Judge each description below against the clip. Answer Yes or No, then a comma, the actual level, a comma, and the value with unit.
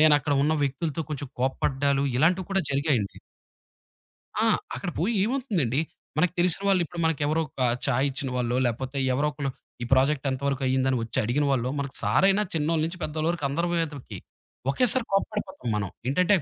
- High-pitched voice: No, medium, 145 Hz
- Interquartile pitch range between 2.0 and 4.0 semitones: No, average, 4.4 semitones